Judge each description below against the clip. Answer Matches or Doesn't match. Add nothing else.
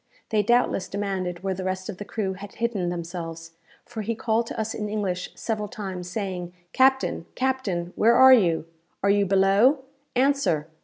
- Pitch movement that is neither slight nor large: Matches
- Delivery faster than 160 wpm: Matches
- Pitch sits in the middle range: Doesn't match